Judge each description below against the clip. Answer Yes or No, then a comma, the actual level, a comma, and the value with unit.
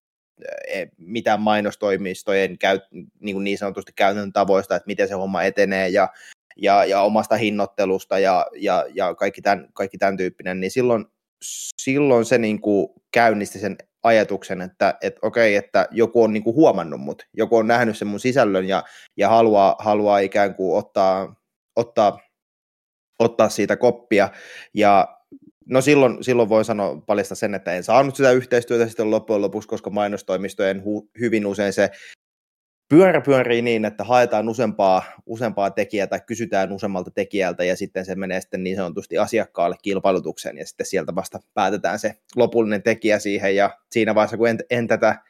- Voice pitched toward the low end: Yes, low, 105 Hz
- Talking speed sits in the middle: No, fast, 160 wpm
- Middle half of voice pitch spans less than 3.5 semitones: Yes, average, 3.0 semitones